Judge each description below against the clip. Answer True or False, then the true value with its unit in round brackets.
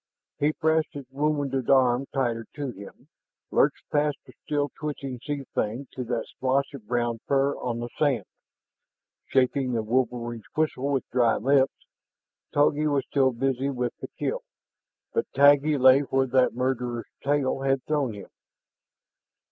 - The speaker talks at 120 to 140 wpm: False (150 wpm)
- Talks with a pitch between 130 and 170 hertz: True (135 Hz)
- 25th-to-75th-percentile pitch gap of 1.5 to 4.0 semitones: True (2.6 semitones)